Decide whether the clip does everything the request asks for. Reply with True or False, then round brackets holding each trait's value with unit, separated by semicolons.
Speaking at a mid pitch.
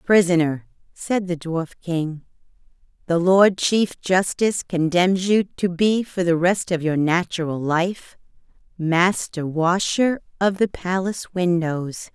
True (180 Hz)